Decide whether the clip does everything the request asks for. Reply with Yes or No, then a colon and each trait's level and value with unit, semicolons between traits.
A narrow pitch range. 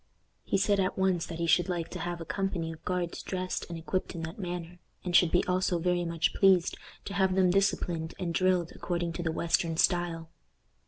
Yes: narrow, 1.8 semitones